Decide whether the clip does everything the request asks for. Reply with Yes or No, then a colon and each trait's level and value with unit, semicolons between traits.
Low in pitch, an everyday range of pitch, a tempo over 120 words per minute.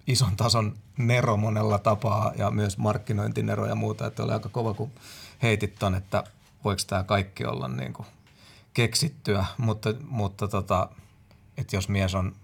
No: low, 105 Hz; narrow, 2.0 semitones; average, 150 wpm